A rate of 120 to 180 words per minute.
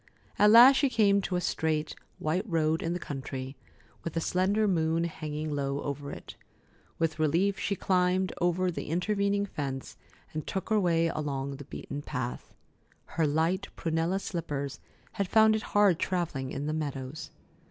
Yes: average, 160 wpm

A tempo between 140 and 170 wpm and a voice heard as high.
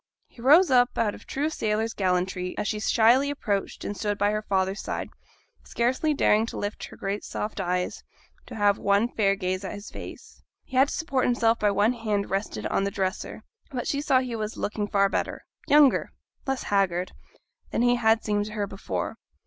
No: average, 195 wpm; high, 210 Hz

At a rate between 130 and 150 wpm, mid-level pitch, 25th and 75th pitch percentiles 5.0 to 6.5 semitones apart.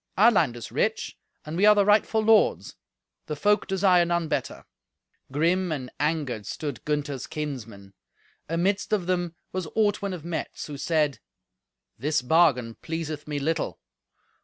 No: average, 145 wpm; medium, 160 Hz; average, 4.3 semitones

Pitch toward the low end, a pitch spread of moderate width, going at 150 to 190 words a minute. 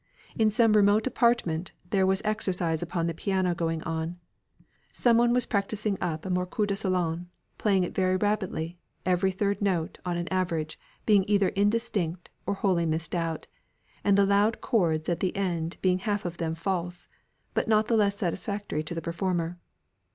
No: medium, 185 Hz; average, 3.2 semitones; average, 170 wpm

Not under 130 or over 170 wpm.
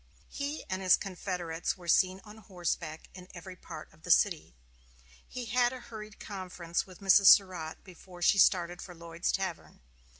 Yes: average, 165 wpm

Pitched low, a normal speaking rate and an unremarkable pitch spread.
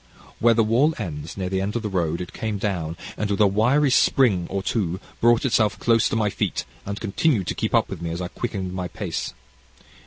No: low, 100 Hz; fast, 225 wpm; average, 3.9 semitones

